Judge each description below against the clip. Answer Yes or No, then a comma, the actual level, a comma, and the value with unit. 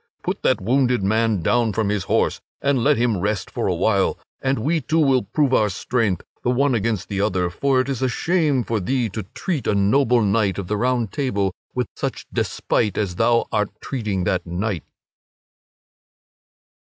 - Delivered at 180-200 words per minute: Yes, average, 185 wpm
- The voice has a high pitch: No, low, 115 Hz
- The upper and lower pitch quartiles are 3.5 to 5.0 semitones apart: Yes, average, 4.4 semitones